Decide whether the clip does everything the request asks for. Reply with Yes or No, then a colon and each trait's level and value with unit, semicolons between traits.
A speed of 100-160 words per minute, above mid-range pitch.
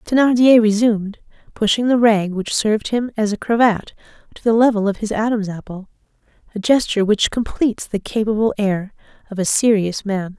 No: average, 170 wpm; high, 215 Hz